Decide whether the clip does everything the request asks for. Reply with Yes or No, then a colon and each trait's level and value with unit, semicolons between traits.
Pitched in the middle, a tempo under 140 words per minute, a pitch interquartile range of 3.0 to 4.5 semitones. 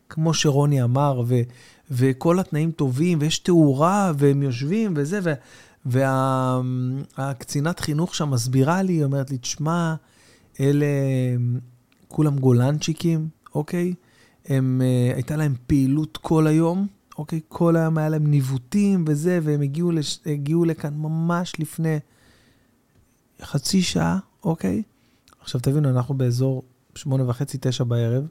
Yes: medium, 145 Hz; average, 125 wpm; average, 3.9 semitones